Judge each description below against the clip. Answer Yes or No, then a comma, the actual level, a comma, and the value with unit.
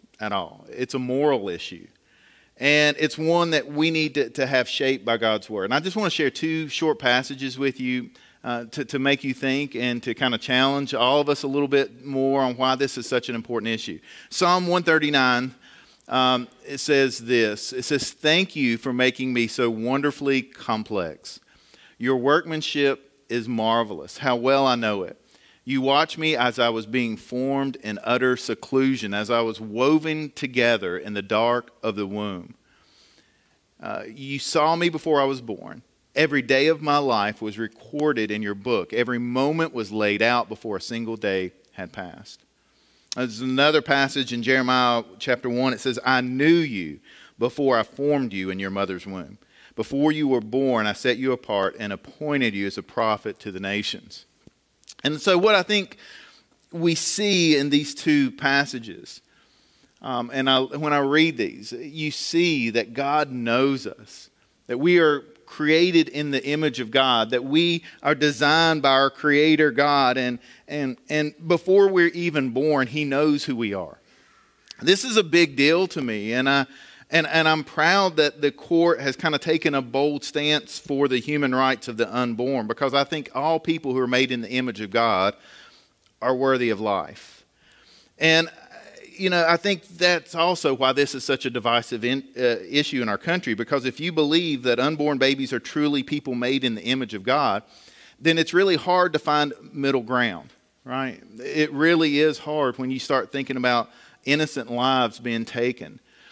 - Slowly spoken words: No, average, 185 wpm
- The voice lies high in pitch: No, low, 135 Hz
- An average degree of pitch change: Yes, average, 3.6 semitones